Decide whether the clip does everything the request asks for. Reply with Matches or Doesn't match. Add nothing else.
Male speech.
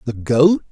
Matches